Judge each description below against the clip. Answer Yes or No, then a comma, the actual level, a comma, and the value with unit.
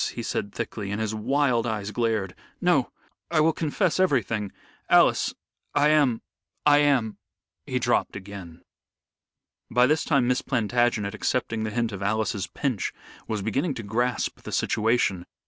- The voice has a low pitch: Yes, low, 115 Hz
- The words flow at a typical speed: Yes, average, 150 wpm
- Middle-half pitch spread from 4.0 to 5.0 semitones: Yes, average, 4.7 semitones